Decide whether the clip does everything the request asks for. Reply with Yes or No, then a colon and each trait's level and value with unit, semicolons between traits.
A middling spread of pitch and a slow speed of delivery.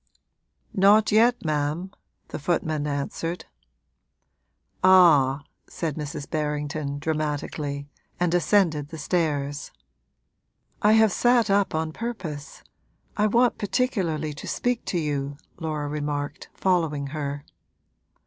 Yes: average, 4.4 semitones; slow, 105 wpm